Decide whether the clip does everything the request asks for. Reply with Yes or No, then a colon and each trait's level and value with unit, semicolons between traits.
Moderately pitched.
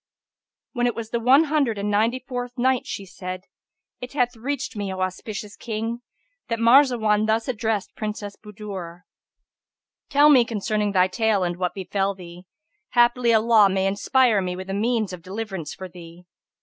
No: high, 215 Hz